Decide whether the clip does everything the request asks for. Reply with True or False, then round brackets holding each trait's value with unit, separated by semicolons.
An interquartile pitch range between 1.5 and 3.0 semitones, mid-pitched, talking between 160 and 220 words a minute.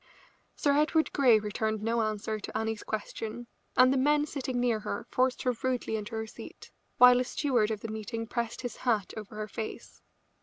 False (2.7 semitones; 225 Hz; 190 wpm)